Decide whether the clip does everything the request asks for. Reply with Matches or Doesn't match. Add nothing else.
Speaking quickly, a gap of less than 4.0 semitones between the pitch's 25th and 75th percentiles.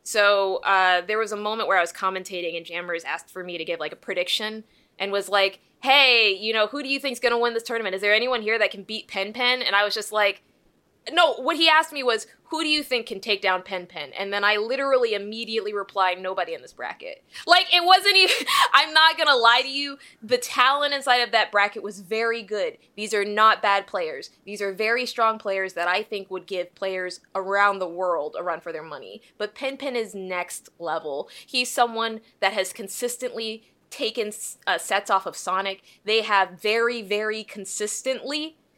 Doesn't match